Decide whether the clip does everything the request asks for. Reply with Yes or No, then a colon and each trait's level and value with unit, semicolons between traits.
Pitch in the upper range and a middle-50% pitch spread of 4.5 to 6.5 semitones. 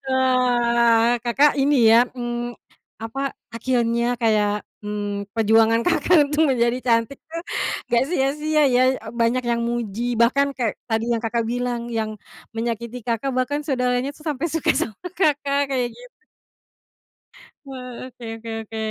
No: high, 240 Hz; average, 2.8 semitones